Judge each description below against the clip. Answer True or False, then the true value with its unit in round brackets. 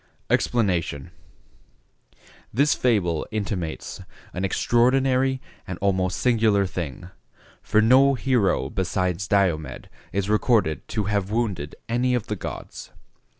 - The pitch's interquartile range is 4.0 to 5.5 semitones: True (4.9 semitones)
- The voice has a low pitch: True (100 Hz)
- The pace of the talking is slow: True (105 wpm)